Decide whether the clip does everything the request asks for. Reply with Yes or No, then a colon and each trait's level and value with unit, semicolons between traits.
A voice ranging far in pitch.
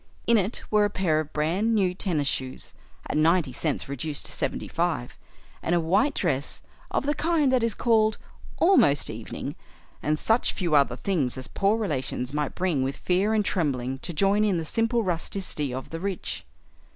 Yes: wide, 6.4 semitones